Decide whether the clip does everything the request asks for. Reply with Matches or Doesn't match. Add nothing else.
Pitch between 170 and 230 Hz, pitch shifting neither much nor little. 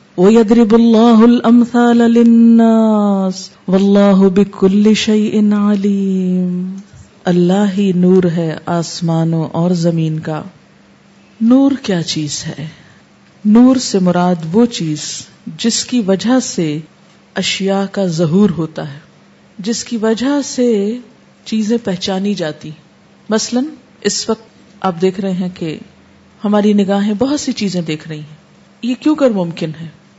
Matches